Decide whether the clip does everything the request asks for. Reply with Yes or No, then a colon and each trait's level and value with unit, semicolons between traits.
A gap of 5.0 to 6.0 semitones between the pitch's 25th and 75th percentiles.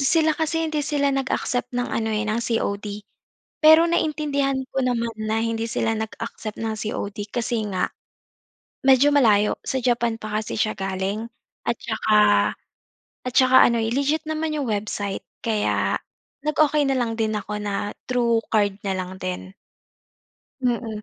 No: average, 4.2 semitones